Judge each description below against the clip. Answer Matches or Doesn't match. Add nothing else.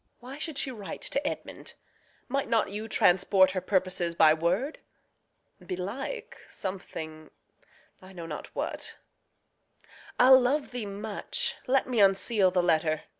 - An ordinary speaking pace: Doesn't match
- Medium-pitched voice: Doesn't match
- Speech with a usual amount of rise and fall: Doesn't match